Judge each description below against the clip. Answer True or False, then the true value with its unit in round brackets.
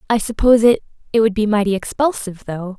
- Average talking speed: True (170 wpm)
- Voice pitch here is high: True (215 Hz)